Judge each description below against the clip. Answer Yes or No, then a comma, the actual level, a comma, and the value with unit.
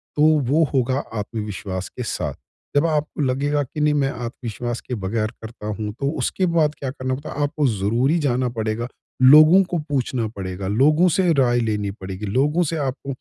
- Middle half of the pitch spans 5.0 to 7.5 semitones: Yes, average, 5.3 semitones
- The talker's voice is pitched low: Yes, low, 130 Hz